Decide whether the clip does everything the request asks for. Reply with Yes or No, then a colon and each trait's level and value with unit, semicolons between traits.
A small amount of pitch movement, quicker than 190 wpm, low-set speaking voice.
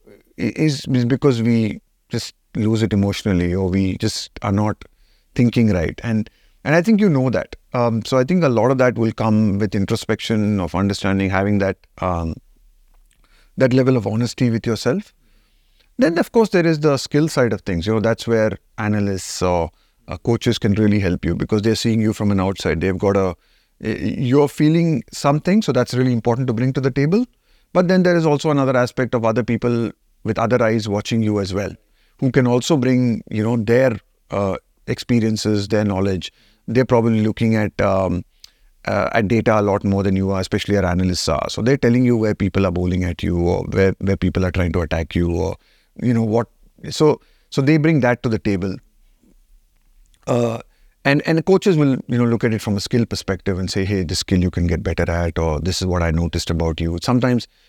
No: average, 4.5 semitones; fast, 205 wpm; low, 110 Hz